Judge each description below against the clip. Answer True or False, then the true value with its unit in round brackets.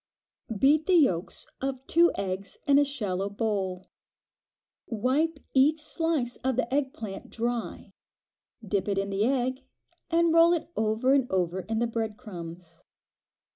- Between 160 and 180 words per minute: False (140 wpm)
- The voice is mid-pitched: False (240 Hz)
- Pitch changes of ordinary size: False (6.2 semitones)